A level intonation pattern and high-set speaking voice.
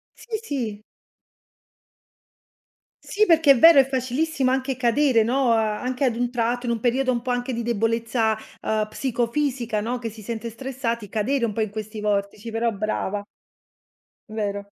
No: average, 3.0 semitones; high, 235 Hz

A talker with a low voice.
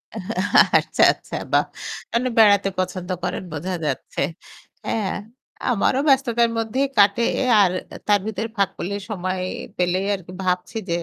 No: high, 200 Hz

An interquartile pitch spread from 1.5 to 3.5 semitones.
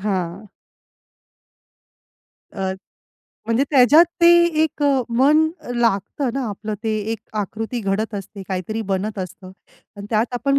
No: average, 4.6 semitones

